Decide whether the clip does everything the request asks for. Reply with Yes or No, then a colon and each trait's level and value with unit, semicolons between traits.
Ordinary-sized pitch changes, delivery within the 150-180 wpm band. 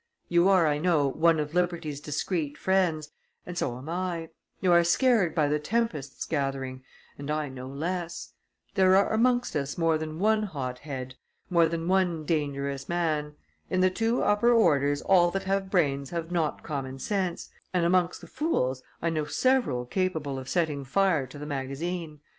Yes: average, 4.4 semitones; average, 175 wpm